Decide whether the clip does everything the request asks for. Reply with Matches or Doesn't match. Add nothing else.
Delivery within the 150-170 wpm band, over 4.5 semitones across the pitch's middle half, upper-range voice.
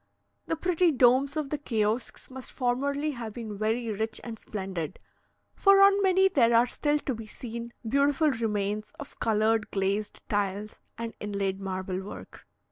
Matches